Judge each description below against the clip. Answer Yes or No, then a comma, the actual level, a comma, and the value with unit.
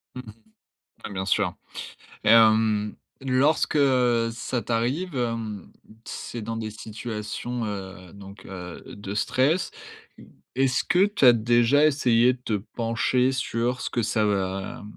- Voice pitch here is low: Yes, low, 115 Hz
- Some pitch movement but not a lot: Yes, average, 3.3 semitones